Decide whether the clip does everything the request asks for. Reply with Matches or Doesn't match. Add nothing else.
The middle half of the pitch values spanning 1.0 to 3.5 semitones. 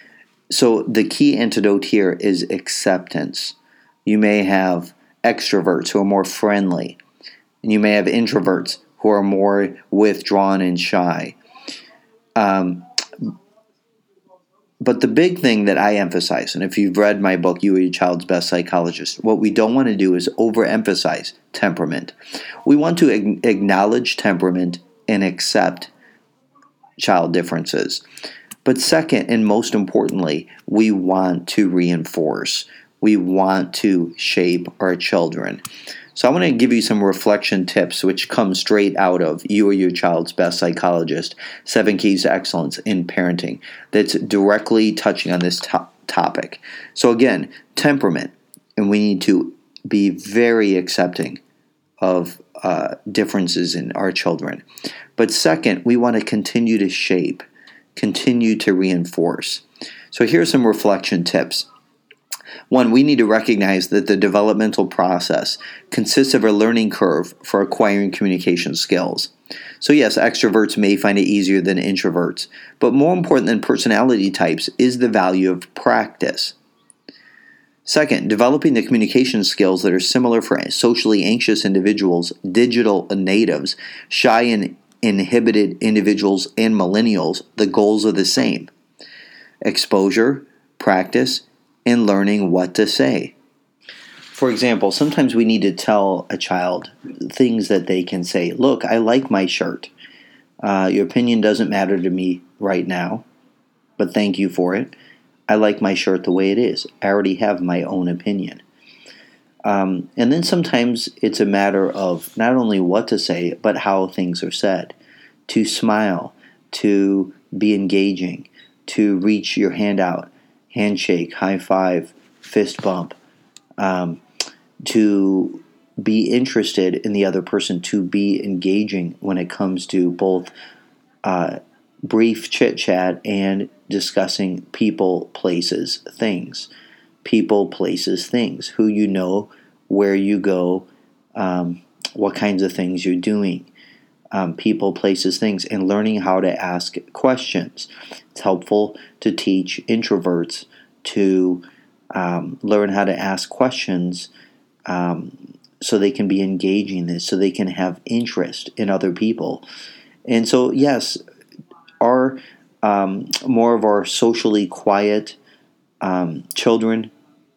Matches